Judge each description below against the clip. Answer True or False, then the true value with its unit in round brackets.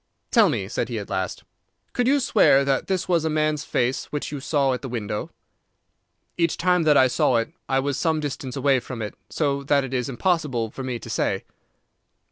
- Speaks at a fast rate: True (210 wpm)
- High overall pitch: False (140 Hz)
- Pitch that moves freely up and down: False (3.4 semitones)